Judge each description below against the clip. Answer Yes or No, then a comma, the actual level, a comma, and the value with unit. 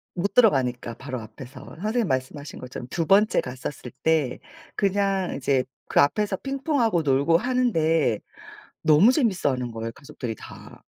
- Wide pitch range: Yes, wide, 8.0 semitones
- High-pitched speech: No, medium, 155 Hz